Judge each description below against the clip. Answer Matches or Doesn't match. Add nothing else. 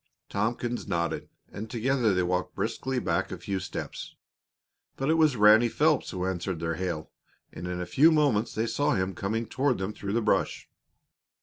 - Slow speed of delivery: Doesn't match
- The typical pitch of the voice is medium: Doesn't match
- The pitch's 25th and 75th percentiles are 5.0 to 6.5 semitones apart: Matches